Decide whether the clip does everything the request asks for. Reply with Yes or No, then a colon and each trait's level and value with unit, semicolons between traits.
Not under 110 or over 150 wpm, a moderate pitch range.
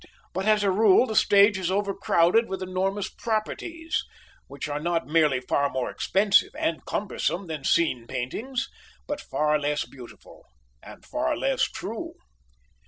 No: average, 145 wpm; wide, 5.7 semitones